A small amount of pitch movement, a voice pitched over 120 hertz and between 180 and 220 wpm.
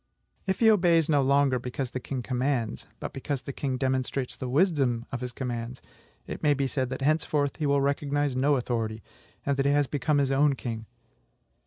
Yes: narrow, 2.3 semitones; low, 135 Hz; average, 195 wpm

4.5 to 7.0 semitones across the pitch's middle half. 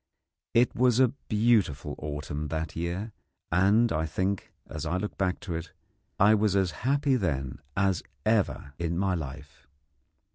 Yes: average, 5.3 semitones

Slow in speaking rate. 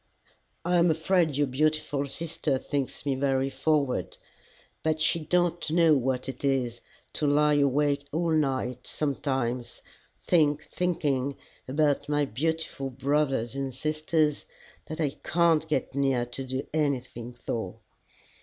Yes: slow, 125 wpm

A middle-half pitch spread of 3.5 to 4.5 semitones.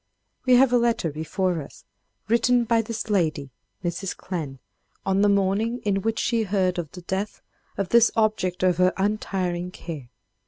Yes: average, 3.9 semitones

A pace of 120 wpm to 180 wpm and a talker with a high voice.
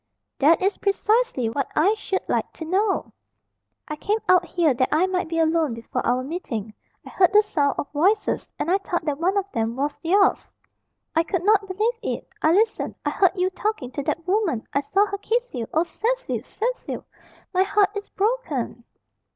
No: average, 190 wpm; very high, 365 Hz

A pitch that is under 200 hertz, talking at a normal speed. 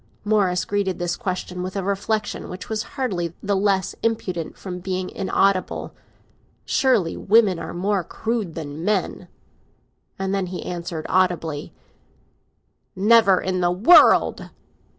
No: high, 190 Hz; slow, 130 wpm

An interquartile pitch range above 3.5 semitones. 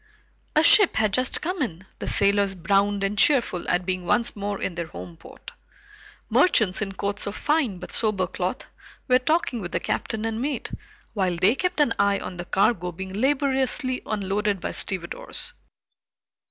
Yes: average, 5.1 semitones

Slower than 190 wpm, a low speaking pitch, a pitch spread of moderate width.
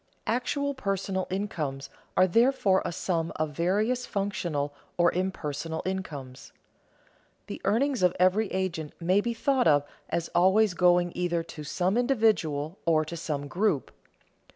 No: slow, 135 wpm; medium, 185 Hz; average, 4.3 semitones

